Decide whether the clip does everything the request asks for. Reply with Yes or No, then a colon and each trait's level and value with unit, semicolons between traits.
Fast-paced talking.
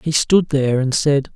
Yes: fast, 220 wpm